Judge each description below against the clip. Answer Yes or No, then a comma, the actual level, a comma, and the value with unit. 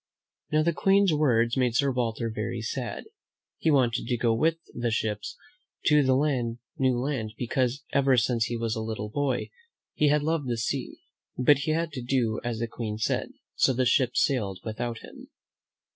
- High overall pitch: No, low, 125 Hz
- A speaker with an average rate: Yes, average, 180 wpm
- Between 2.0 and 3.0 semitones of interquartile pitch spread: No, average, 3.5 semitones